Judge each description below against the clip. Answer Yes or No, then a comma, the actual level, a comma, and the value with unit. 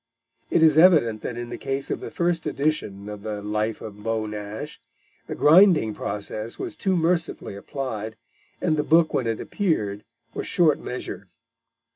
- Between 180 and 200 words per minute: No, average, 165 wpm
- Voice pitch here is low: Yes, low, 120 Hz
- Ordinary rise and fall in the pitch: No, wide, 7.1 semitones